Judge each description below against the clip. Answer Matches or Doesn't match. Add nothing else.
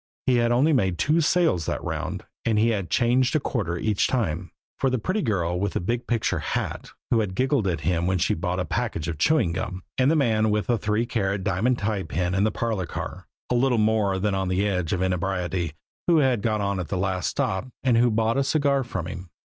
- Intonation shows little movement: Doesn't match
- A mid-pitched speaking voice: Doesn't match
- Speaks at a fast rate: Matches